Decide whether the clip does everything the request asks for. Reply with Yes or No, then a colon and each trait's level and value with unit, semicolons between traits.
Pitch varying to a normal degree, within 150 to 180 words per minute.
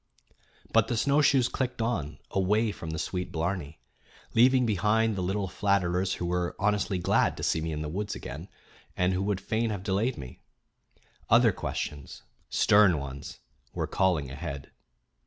Yes: average, 4.6 semitones; average, 155 wpm